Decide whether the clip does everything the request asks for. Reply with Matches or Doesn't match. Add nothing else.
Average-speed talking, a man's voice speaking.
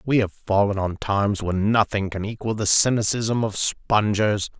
Matches